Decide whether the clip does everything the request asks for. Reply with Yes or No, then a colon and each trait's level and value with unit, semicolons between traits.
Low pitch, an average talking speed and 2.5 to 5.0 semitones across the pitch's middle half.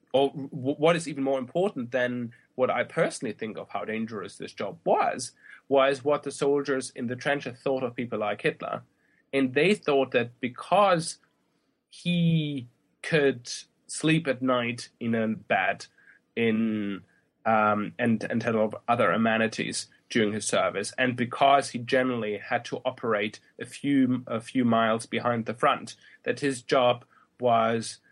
Yes: low, 125 Hz; average, 150 wpm; average, 3.5 semitones